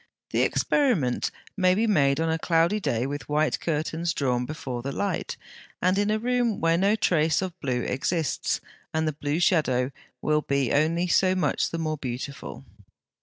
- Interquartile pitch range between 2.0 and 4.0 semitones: No, average, 4.8 semitones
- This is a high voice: No, medium, 160 Hz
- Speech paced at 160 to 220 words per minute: Yes, average, 170 wpm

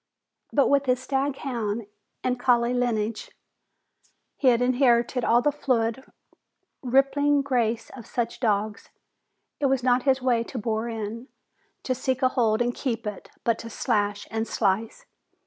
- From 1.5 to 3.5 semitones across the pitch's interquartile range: Yes, narrow, 2.6 semitones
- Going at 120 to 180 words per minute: Yes, average, 145 wpm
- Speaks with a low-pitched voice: No, high, 245 Hz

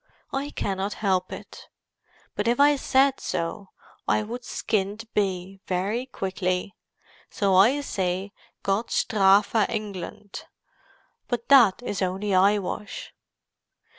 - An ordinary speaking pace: No, slow, 110 wpm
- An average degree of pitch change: Yes, average, 3.3 semitones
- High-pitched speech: Yes, high, 205 Hz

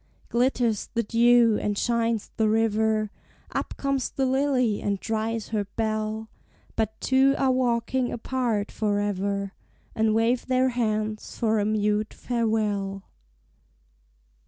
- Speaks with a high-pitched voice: Yes, high, 220 Hz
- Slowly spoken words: Yes, slow, 120 wpm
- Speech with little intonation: Yes, narrow, 2.2 semitones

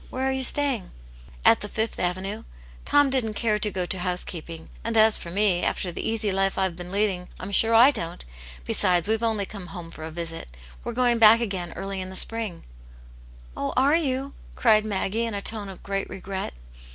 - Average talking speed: No, fast, 215 wpm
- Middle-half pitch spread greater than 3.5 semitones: Yes, average, 4.1 semitones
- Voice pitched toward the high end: Yes, high, 200 Hz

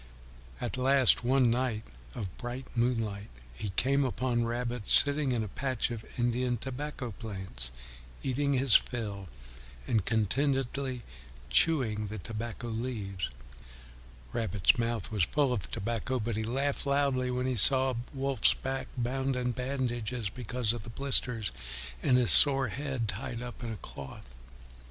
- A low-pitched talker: Yes, low, 120 Hz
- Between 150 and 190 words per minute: No, average, 140 wpm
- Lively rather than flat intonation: No, average, 3.1 semitones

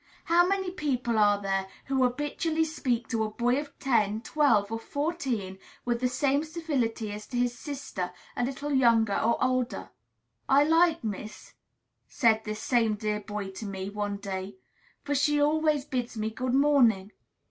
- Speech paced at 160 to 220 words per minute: Yes, average, 170 wpm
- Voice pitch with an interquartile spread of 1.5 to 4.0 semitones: No, average, 5.2 semitones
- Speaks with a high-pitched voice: Yes, high, 245 Hz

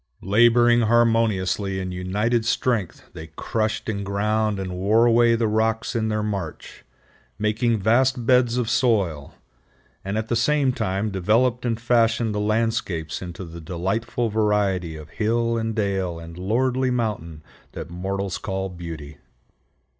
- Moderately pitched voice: No, low, 110 Hz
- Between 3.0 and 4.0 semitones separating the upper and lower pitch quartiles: Yes, average, 3.7 semitones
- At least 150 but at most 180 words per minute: No, average, 140 wpm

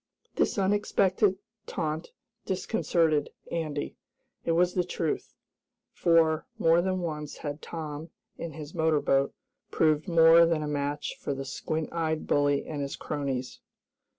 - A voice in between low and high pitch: Yes, medium, 160 Hz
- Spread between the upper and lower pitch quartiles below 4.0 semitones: Yes, narrow, 2.5 semitones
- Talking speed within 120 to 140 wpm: Yes, slow, 135 wpm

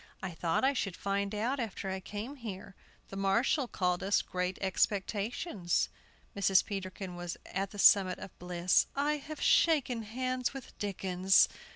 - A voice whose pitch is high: Yes, high, 200 Hz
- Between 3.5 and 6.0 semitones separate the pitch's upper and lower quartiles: Yes, average, 4.4 semitones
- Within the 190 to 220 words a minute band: No, average, 155 wpm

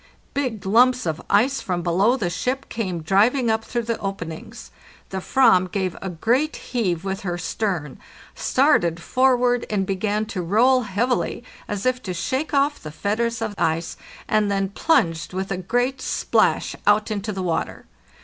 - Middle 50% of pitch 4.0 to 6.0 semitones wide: Yes, average, 5.1 semitones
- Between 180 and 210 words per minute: No, average, 165 wpm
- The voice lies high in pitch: Yes, high, 205 Hz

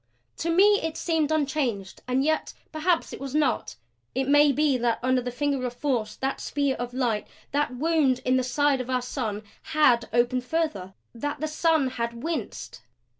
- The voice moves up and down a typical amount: Yes, average, 3.9 semitones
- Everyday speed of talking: Yes, average, 180 wpm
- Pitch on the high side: Yes, very high, 270 Hz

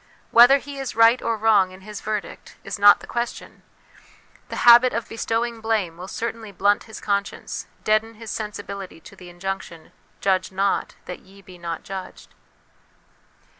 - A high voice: Yes, high, 205 Hz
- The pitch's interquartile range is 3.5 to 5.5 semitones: No, average, 3.1 semitones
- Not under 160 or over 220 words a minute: Yes, average, 165 wpm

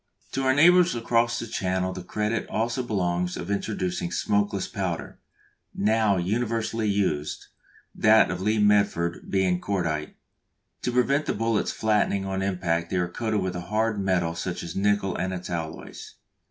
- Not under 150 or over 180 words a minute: Yes, average, 160 wpm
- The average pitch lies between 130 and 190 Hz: No, low, 100 Hz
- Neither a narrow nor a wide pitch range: Yes, average, 3.7 semitones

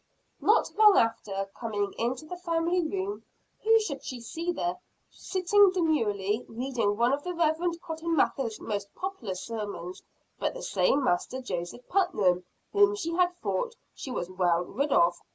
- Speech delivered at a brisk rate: No, average, 155 wpm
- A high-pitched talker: Yes, very high, 280 Hz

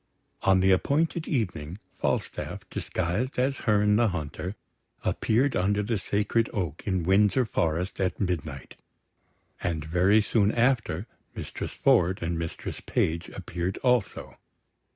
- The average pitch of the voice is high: No, very low, 95 Hz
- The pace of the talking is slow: Yes, slow, 125 wpm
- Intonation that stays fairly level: No, average, 4.4 semitones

